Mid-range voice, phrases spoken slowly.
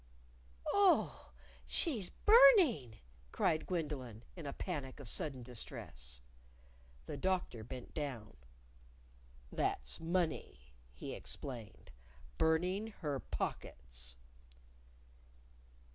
Yes: medium, 145 Hz; slow, 85 wpm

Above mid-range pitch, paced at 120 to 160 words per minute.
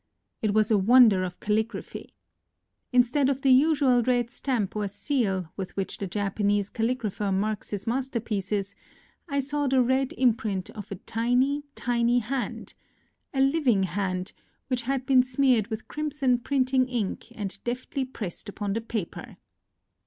Yes: high, 235 Hz; average, 150 wpm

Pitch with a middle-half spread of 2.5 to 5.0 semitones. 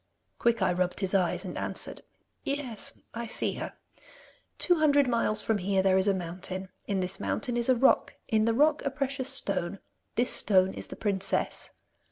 No: wide, 5.4 semitones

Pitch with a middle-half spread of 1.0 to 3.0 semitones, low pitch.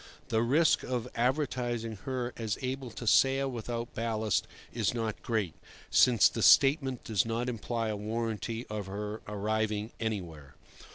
Yes: narrow, 2.5 semitones; low, 115 Hz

